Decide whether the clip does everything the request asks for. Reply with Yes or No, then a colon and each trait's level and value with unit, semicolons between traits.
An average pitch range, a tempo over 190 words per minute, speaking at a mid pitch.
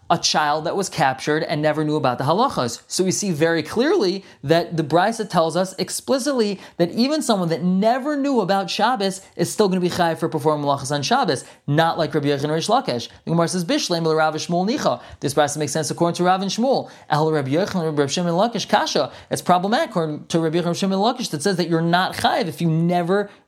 Yes: average, 3.7 semitones; fast, 205 wpm; medium, 170 Hz